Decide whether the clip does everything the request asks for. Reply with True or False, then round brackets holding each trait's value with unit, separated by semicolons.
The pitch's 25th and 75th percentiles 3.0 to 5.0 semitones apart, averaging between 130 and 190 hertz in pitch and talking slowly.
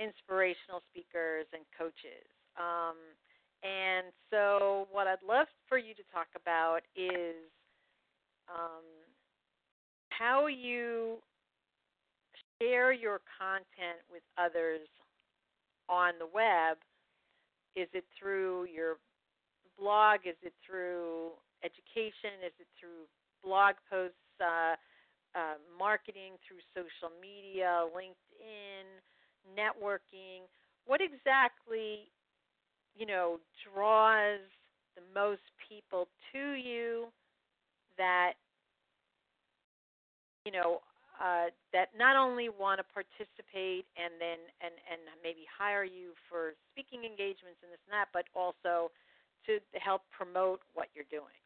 True (3.4 semitones; 185 Hz; 105 wpm)